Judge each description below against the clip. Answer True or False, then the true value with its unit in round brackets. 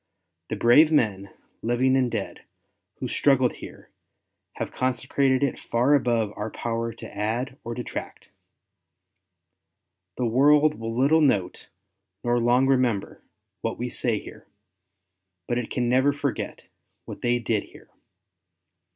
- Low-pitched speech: True (125 Hz)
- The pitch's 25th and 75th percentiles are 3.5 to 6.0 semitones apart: False (2.6 semitones)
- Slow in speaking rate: True (130 wpm)